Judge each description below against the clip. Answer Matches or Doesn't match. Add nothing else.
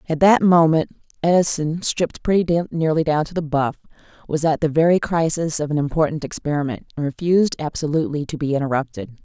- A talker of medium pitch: Matches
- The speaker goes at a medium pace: Matches